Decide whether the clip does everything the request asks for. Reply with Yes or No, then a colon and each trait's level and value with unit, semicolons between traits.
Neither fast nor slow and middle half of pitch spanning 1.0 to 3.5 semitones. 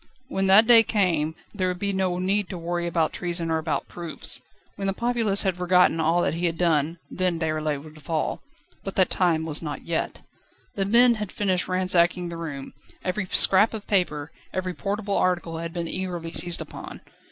Yes: average, 190 wpm; average, 2.8 semitones